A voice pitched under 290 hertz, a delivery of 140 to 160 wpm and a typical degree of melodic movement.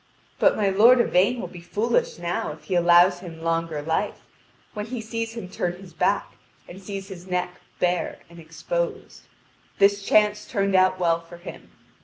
No: medium, 185 Hz; average, 175 wpm; average, 3.2 semitones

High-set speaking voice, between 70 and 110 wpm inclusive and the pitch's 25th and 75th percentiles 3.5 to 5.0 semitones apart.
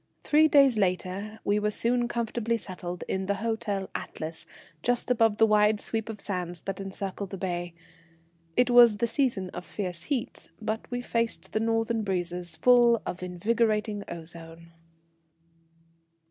No: high, 210 Hz; average, 145 wpm; average, 4.1 semitones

